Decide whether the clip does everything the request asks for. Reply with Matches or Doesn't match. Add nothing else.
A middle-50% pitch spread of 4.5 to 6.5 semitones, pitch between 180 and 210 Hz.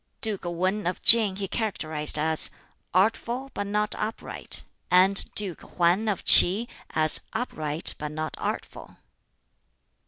Matches